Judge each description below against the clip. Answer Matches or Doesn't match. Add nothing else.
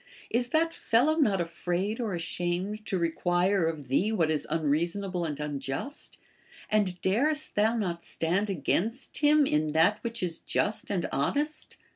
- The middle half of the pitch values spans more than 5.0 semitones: Matches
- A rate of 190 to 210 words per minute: Doesn't match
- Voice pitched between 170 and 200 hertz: Matches